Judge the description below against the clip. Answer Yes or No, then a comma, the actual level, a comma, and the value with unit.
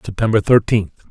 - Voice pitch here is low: Yes, low, 110 Hz